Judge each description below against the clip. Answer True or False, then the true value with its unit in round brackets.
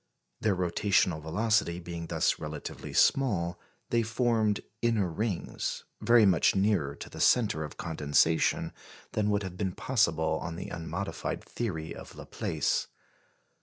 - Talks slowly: True (130 wpm)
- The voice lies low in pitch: True (95 Hz)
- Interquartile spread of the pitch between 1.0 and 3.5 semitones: False (4.7 semitones)